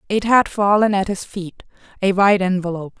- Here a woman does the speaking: Yes, female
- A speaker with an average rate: Yes, average, 160 wpm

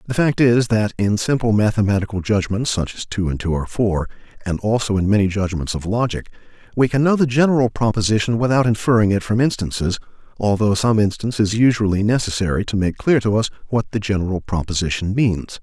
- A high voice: No, low, 105 Hz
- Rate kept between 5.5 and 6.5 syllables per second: Yes, 6.1 syllables/s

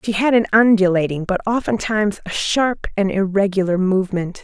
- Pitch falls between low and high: No, high, 200 Hz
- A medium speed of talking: Yes, average, 150 wpm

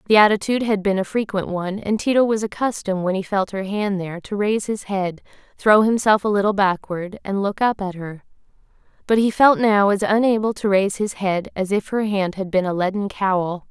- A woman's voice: Yes, female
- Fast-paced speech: Yes, fast, 220 wpm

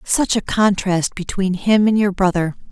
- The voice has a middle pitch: No, high, 195 Hz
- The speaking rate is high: No, average, 175 wpm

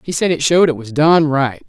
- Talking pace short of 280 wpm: No, fast, 285 wpm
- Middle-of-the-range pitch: Yes, medium, 150 Hz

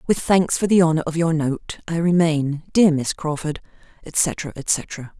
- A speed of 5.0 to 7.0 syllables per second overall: No, 4.1 syllables/s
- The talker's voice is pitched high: No, medium, 160 Hz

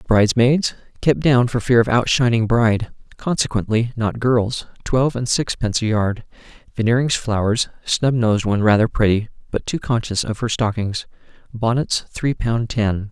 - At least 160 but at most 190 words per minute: No, average, 150 wpm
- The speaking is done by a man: Yes, male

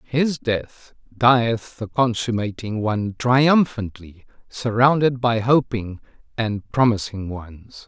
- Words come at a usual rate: No, slow, 100 wpm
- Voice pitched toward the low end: Yes, low, 115 Hz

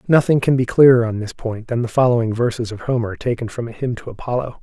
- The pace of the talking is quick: Yes, fast, 245 wpm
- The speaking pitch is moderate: No, low, 120 Hz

